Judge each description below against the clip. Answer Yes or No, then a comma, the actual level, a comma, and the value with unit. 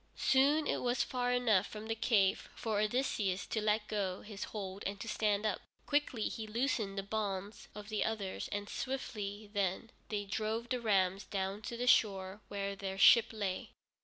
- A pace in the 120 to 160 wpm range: No, average, 180 wpm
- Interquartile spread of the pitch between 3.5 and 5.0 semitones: No, narrow, 2.4 semitones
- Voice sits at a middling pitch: No, high, 210 Hz